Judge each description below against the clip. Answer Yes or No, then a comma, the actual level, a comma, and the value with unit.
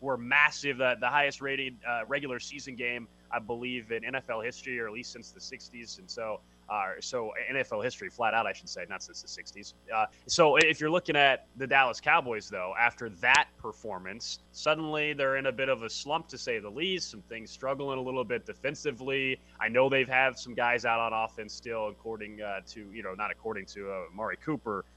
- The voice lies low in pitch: Yes, low, 130 Hz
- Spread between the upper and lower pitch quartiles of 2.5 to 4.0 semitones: Yes, average, 3.5 semitones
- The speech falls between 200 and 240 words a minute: Yes, fast, 205 wpm